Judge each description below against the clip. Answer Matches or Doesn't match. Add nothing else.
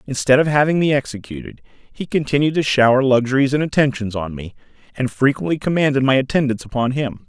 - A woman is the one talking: Doesn't match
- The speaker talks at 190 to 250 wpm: Doesn't match